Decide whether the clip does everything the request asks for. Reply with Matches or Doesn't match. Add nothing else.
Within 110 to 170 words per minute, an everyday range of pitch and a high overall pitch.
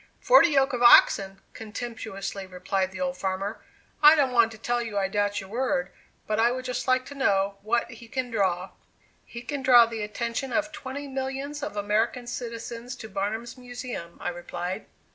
Doesn't match